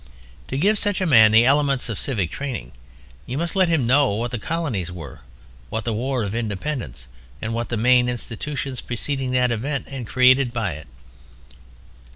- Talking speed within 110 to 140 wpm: No, average, 180 wpm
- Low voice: Yes, low, 125 Hz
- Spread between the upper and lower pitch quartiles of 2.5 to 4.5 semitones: Yes, average, 3.9 semitones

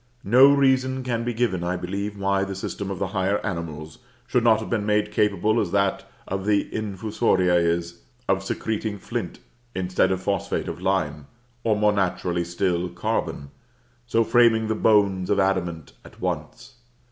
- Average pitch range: Yes, average, 3.3 semitones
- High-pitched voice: No, low, 100 Hz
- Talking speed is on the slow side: No, average, 165 wpm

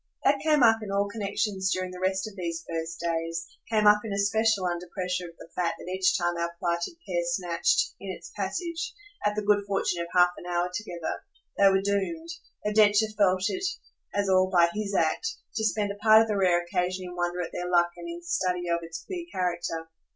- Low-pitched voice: No, high, 190 Hz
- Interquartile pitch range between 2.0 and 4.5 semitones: Yes, average, 3.4 semitones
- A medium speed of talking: No, fast, 215 wpm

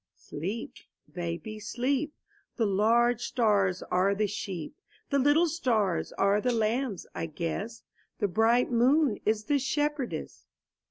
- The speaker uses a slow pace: Yes, slow, 130 wpm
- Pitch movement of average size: Yes, average, 4.3 semitones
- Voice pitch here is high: Yes, high, 225 Hz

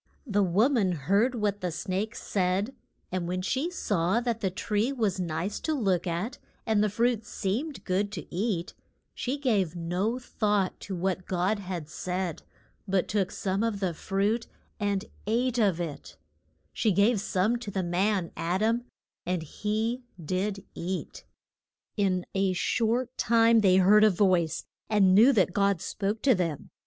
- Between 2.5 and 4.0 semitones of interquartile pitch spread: Yes, average, 3.4 semitones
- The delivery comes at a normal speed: Yes, average, 165 wpm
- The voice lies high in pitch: Yes, high, 200 Hz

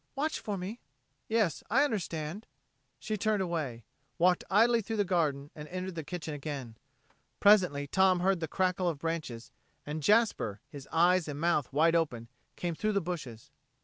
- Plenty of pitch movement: No, average, 4.9 semitones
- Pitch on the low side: No, medium, 170 Hz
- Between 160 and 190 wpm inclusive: Yes, average, 165 wpm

